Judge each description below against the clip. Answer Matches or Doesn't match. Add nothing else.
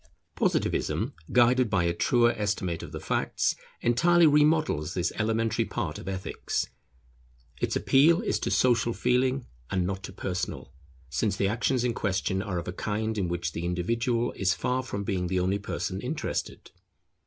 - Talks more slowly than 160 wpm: Doesn't match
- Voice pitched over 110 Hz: Doesn't match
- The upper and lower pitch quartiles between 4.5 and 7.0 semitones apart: Matches